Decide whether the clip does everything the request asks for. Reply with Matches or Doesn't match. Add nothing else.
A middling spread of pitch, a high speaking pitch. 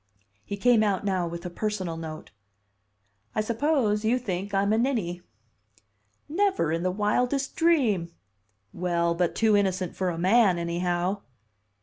Matches